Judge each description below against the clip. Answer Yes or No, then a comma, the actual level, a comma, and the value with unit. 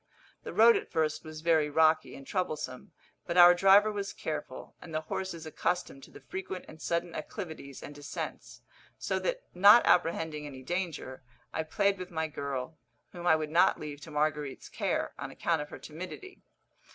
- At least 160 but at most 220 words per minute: Yes, average, 175 wpm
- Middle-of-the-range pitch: Yes, medium, 160 Hz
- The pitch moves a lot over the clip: No, average, 3.5 semitones